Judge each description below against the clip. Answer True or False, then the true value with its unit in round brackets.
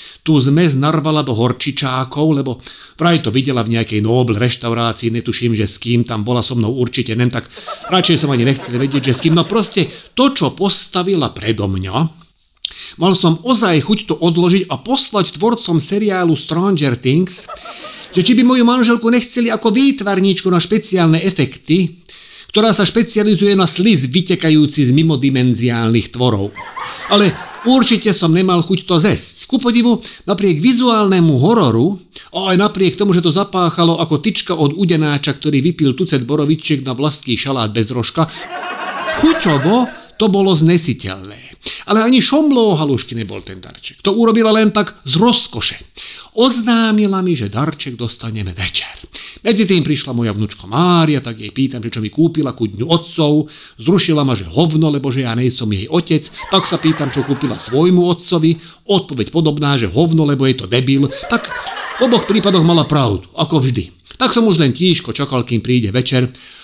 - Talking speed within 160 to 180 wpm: True (165 wpm)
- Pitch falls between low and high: True (160 Hz)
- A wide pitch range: True (7.4 semitones)